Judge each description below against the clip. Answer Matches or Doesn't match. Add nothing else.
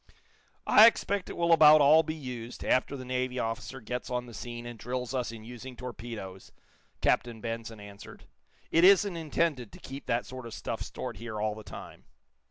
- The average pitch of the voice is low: Matches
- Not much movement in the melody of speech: Doesn't match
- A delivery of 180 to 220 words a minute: Matches